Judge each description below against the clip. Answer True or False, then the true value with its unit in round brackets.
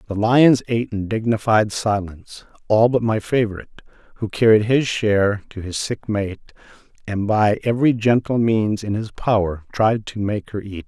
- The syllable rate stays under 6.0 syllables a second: True (5.0 syllables/s)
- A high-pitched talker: False (110 Hz)